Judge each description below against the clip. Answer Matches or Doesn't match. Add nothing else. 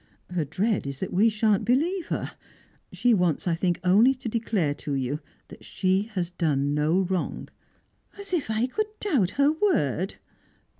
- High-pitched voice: Matches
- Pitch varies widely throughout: Matches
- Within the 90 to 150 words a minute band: Doesn't match